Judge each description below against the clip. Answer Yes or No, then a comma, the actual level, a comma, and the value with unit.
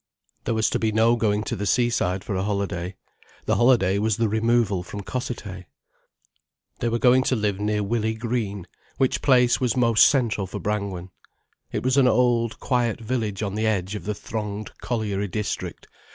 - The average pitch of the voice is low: Yes, low, 110 Hz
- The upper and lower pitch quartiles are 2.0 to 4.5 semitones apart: Yes, average, 2.8 semitones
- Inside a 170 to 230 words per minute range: Yes, average, 180 wpm